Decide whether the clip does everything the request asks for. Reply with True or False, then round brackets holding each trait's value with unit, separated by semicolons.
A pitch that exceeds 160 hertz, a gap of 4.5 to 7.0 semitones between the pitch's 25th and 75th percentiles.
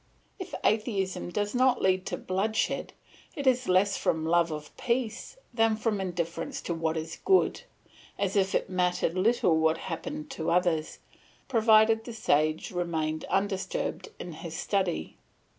True (190 Hz; 5.1 semitones)